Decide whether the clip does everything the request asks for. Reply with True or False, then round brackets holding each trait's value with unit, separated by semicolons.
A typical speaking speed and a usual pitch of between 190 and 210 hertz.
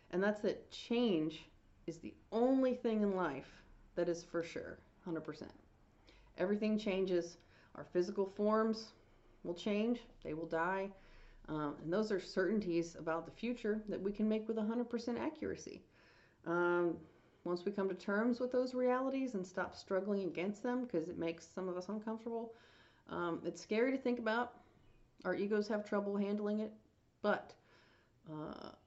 True (155 wpm; 195 Hz)